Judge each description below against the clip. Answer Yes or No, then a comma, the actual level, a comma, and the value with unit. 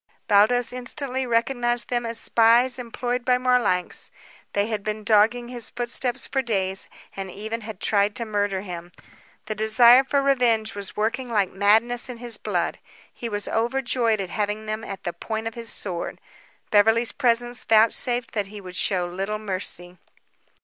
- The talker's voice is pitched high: Yes, high, 225 Hz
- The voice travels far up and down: No, average, 2.9 semitones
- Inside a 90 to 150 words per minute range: No, average, 165 wpm